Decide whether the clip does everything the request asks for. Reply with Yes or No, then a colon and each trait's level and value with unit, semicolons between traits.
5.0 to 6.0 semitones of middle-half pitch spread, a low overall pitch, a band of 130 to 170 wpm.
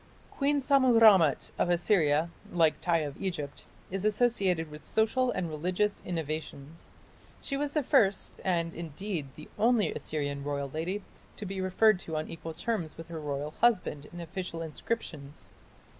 No: wide, 5.4 semitones; medium, 175 Hz; average, 155 wpm